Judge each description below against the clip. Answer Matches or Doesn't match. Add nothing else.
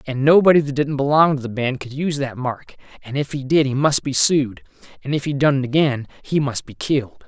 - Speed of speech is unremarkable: Doesn't match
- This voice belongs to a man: Matches